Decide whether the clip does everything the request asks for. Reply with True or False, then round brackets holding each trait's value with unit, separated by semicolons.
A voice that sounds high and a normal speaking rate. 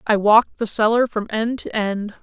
False (220 Hz; 215 wpm)